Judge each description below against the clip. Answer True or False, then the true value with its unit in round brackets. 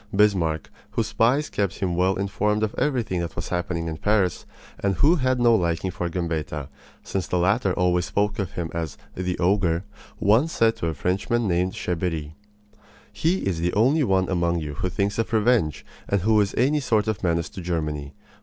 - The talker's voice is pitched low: True (95 Hz)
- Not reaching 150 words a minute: False (190 wpm)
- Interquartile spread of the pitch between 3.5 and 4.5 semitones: True (4.0 semitones)